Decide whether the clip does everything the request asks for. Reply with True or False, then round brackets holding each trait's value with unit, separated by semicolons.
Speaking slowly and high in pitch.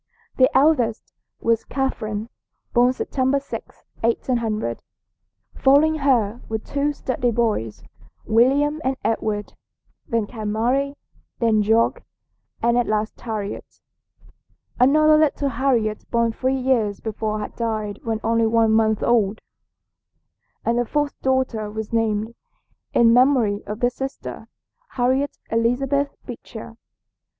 True (120 wpm; 235 Hz)